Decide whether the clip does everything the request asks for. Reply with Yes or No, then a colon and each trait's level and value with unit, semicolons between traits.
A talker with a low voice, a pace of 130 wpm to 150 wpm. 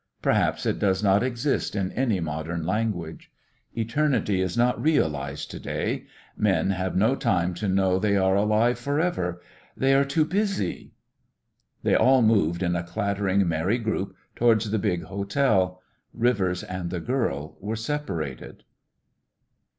Yes: low, 100 Hz; average, 145 wpm